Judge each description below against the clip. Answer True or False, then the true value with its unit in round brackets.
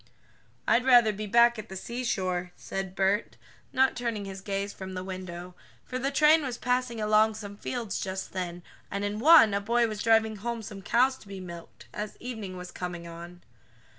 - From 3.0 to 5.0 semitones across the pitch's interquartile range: True (4.0 semitones)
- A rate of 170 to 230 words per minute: True (190 wpm)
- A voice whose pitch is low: False (210 Hz)